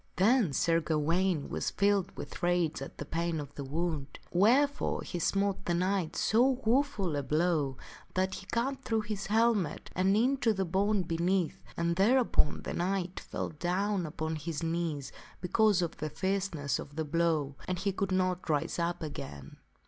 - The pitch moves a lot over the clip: No, average, 3.9 semitones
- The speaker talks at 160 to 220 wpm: Yes, average, 170 wpm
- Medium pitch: Yes, medium, 175 Hz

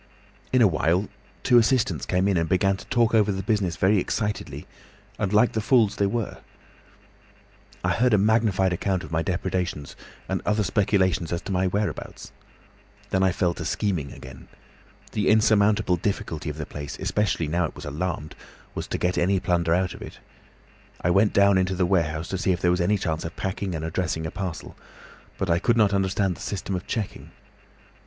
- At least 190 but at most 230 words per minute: Yes, average, 195 wpm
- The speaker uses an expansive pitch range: No, average, 3.2 semitones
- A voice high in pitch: No, very low, 95 Hz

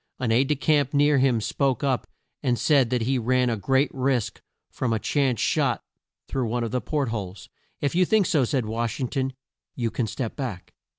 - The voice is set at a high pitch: No, low, 130 Hz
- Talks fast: Yes, fast, 210 wpm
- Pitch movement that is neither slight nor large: Yes, average, 3.1 semitones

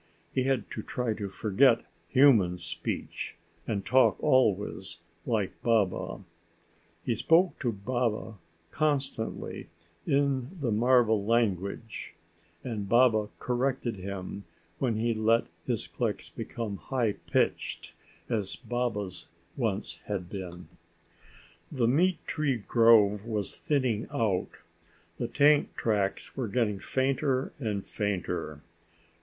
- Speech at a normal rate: No, slow, 110 wpm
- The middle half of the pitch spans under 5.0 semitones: Yes, average, 4.1 semitones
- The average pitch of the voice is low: Yes, low, 115 Hz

